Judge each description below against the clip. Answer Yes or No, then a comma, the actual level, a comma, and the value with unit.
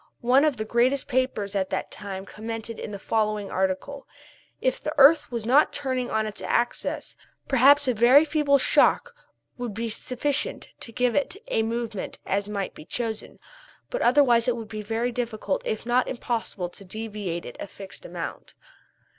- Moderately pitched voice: No, high, 235 Hz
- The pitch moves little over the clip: No, average, 3.7 semitones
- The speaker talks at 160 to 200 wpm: Yes, average, 175 wpm